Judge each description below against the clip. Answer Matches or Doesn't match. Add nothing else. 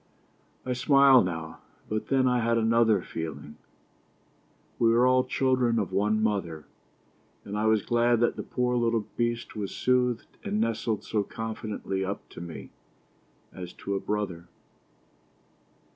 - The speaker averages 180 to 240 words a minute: Doesn't match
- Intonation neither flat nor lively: Matches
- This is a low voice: Matches